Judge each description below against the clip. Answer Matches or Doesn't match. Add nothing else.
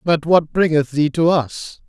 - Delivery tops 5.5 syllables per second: Doesn't match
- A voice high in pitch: Doesn't match